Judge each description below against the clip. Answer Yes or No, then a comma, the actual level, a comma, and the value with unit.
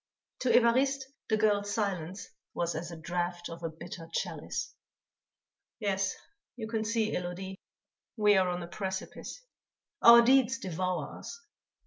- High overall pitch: Yes, high, 195 Hz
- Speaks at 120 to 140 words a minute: Yes, slow, 135 wpm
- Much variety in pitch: No, average, 4.2 semitones